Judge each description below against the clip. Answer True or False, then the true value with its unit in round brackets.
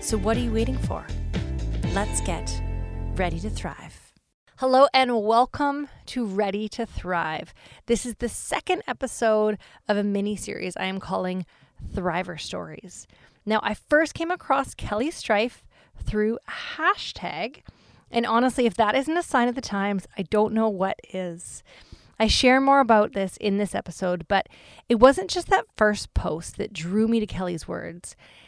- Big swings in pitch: False (4.9 semitones)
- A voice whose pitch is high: True (215 Hz)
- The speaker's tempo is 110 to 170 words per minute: True (160 wpm)